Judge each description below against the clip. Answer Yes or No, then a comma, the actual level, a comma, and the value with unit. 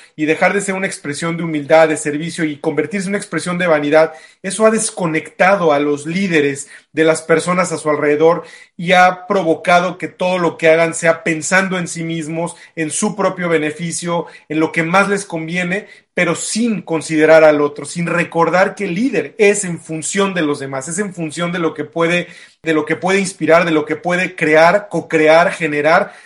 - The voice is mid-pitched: Yes, medium, 165 Hz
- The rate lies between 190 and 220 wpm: Yes, average, 200 wpm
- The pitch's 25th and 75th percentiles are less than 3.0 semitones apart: Yes, narrow, 2.5 semitones